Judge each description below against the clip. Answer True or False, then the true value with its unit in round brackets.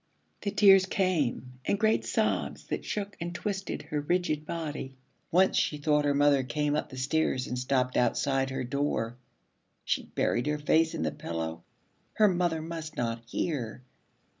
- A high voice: False (150 Hz)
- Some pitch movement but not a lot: True (5.0 semitones)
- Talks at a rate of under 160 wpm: False (165 wpm)